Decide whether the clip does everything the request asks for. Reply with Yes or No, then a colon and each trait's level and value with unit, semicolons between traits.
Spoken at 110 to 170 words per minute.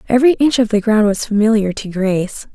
No: fast, 210 wpm